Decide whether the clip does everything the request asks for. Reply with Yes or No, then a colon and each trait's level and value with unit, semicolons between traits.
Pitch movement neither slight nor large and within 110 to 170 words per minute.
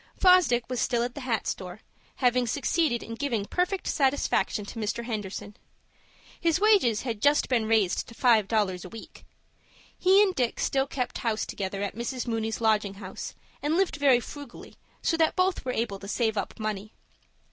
No: average, 5.0 semitones; average, 180 wpm